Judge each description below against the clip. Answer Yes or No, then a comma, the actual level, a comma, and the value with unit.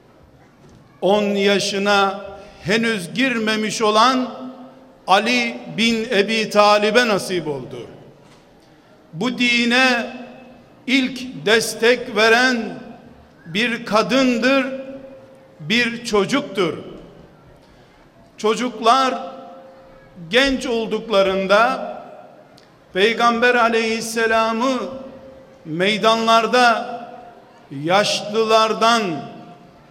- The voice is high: Yes, high, 225 Hz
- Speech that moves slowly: Yes, slow, 55 wpm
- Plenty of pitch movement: No, average, 3.2 semitones